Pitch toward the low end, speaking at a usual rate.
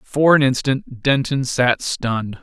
Yes: low, 130 Hz; average, 150 wpm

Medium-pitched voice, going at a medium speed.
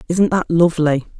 Yes: medium, 165 Hz; average, 150 wpm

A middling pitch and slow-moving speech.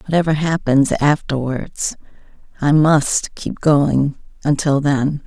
Yes: medium, 145 Hz; slow, 105 wpm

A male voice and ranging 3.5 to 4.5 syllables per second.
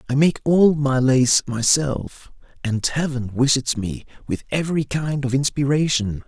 Yes: male; 4.3 syllables/s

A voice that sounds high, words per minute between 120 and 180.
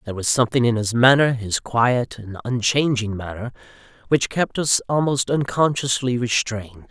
No: low, 120 Hz; average, 150 wpm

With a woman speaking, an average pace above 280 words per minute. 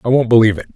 No: male; fast, 315 wpm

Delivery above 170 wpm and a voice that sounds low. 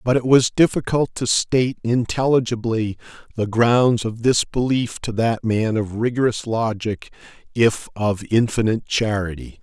No: slow, 135 wpm; low, 115 Hz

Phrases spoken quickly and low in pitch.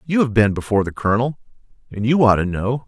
Yes: fast, 230 wpm; low, 115 Hz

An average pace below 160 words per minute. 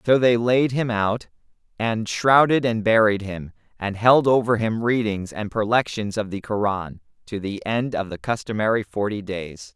No: average, 170 wpm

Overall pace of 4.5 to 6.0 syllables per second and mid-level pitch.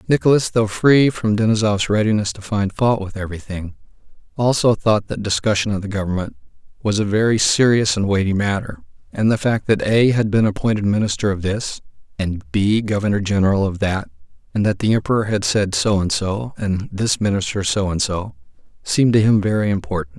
No: 5.5 syllables/s; low, 105 Hz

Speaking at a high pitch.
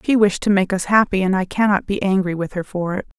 Yes: high, 195 Hz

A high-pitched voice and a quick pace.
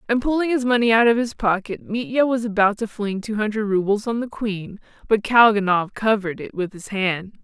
Yes: high, 215 Hz; fast, 210 wpm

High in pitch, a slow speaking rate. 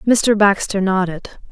Yes: high, 200 Hz; slow, 120 wpm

